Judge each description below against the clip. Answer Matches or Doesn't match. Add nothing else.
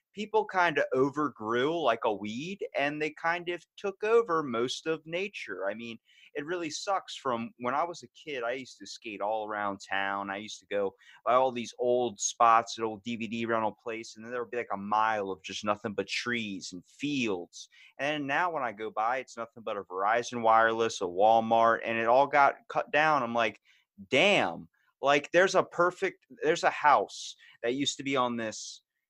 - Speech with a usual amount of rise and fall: Doesn't match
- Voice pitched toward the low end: Matches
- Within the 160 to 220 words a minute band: Matches